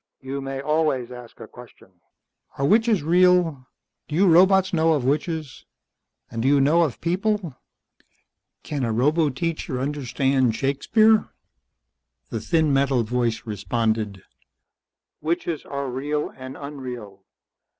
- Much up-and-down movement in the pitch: No, average, 4.7 semitones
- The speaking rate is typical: No, slow, 120 wpm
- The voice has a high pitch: No, medium, 140 Hz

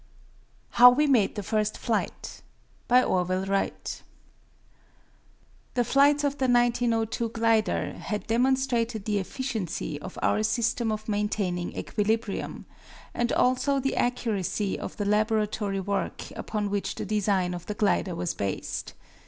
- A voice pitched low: No, high, 215 Hz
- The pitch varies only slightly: No, average, 3.2 semitones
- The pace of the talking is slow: Yes, slow, 130 wpm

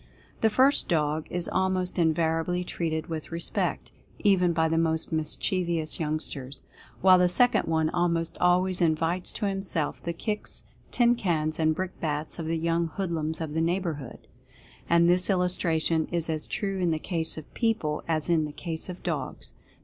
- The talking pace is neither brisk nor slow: Yes, average, 170 wpm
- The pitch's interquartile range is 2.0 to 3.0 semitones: Yes, narrow, 2.4 semitones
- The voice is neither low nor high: Yes, medium, 170 Hz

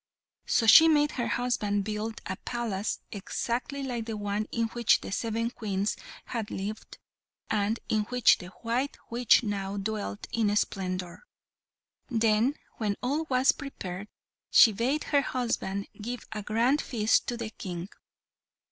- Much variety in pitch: No, average, 3.1 semitones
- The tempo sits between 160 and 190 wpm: No, average, 145 wpm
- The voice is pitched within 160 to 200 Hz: No, high, 225 Hz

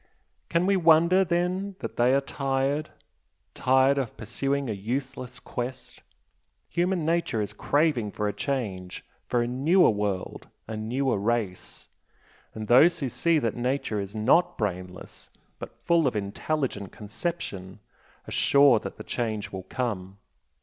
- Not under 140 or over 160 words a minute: Yes, average, 145 wpm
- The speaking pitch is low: Yes, low, 125 Hz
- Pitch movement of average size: No, wide, 6.3 semitones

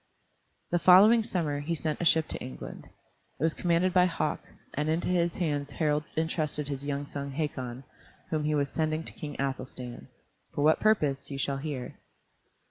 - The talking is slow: No, average, 175 wpm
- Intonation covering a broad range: No, average, 3.0 semitones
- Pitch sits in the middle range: Yes, medium, 150 Hz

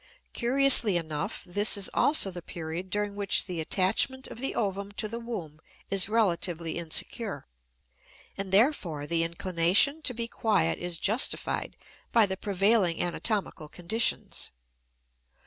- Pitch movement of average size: Yes, average, 4.7 semitones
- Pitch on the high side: Yes, high, 195 Hz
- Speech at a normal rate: No, slow, 130 wpm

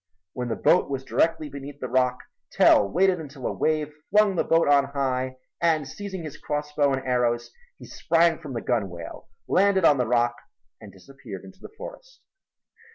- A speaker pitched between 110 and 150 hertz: Yes, medium, 140 Hz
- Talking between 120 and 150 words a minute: No, average, 175 wpm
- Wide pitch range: No, average, 4.7 semitones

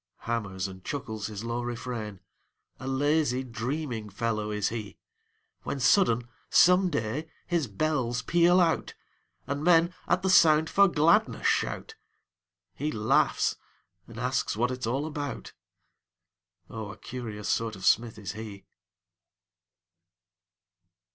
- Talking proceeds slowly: Yes, slow, 125 wpm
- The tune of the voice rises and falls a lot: Yes, wide, 5.9 semitones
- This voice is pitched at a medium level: No, low, 120 Hz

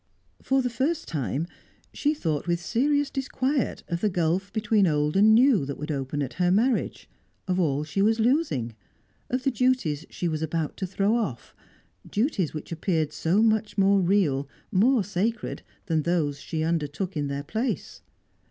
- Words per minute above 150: Yes, average, 170 wpm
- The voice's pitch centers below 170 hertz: No, medium, 185 Hz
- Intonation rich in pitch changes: Yes, wide, 6.5 semitones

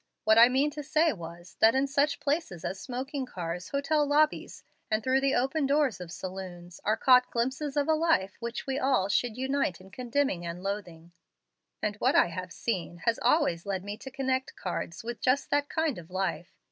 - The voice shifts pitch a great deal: Yes, wide, 6.9 semitones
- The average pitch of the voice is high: Yes, high, 245 Hz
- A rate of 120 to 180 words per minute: No, average, 195 wpm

